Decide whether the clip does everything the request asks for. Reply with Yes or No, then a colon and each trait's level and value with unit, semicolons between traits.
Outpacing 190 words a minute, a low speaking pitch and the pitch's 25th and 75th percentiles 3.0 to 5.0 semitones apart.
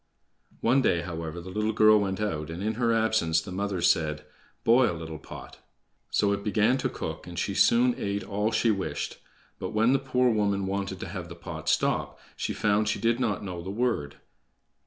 Yes: average, 200 wpm; low, 100 Hz; average, 4.3 semitones